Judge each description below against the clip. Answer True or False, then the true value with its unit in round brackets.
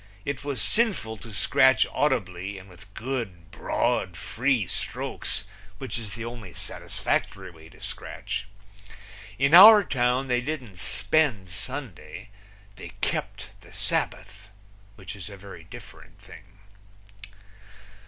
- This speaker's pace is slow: True (125 wpm)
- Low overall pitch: True (110 Hz)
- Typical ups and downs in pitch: False (5.9 semitones)